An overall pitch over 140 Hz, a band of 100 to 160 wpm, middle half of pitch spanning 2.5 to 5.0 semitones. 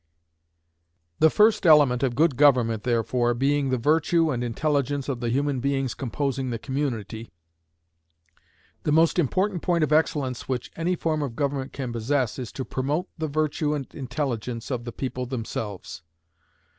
No: low, 135 Hz; average, 155 wpm; average, 3.7 semitones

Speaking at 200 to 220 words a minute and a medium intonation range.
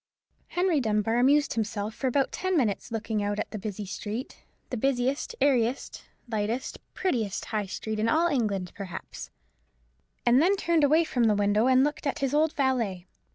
No: average, 165 wpm; average, 4.9 semitones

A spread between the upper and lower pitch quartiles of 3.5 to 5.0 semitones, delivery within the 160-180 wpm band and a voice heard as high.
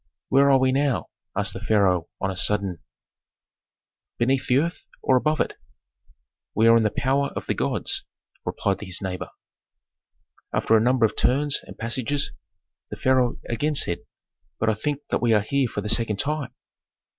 No: average, 4.5 semitones; average, 170 wpm; low, 120 Hz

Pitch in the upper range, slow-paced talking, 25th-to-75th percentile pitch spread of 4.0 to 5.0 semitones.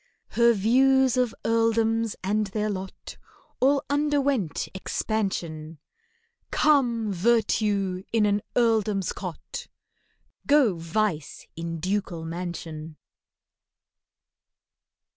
Yes: high, 210 Hz; slow, 85 wpm; average, 4.5 semitones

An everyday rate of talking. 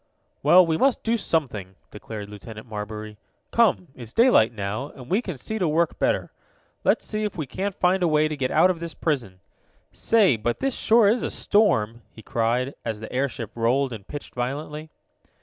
Yes: average, 190 wpm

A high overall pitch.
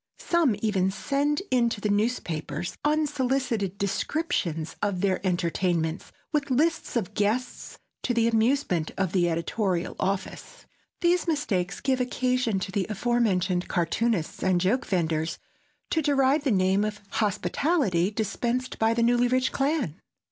Yes: high, 215 Hz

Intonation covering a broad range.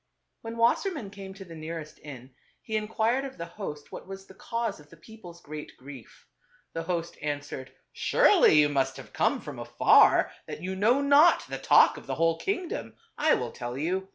Yes: wide, 7.1 semitones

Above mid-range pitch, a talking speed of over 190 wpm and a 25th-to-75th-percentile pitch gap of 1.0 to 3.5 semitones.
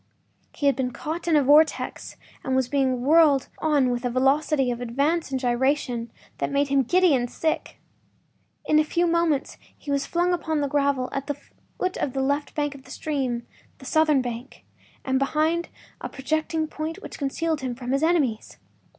No: very high, 280 Hz; average, 175 wpm; average, 3.2 semitones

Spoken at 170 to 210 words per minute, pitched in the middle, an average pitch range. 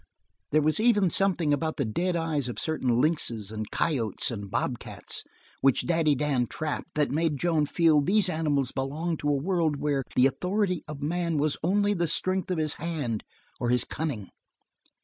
Yes: average, 175 wpm; medium, 155 Hz; average, 3.8 semitones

